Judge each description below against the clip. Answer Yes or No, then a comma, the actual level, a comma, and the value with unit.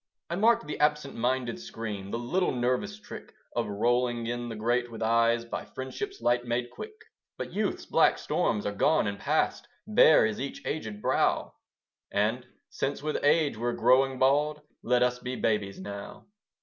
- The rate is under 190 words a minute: Yes, average, 170 wpm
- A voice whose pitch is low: Yes, low, 120 Hz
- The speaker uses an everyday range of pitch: Yes, average, 3.9 semitones